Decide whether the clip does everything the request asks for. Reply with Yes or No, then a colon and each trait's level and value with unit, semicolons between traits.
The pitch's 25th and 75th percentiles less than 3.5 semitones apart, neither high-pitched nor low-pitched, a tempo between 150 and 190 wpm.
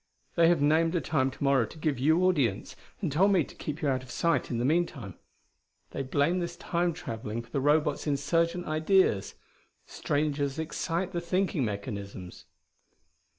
No: average, 4.4 semitones; medium, 150 Hz; average, 170 wpm